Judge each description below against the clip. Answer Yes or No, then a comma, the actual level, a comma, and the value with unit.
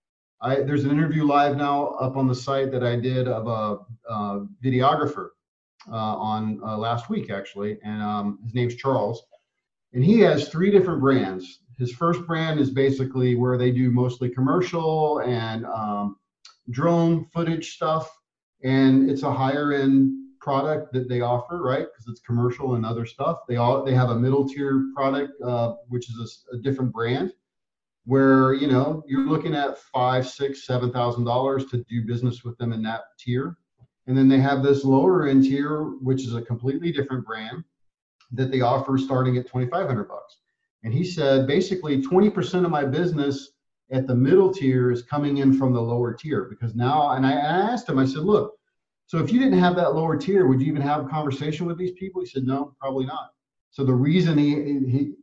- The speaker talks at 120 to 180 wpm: No, average, 195 wpm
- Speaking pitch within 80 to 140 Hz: Yes, low, 135 Hz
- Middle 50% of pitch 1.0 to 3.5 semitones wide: Yes, average, 3.1 semitones